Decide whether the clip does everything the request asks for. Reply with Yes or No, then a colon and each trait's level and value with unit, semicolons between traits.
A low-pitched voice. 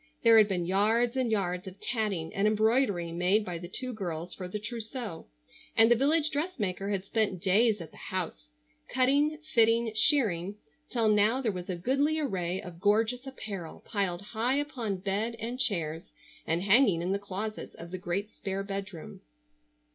No: high, 205 Hz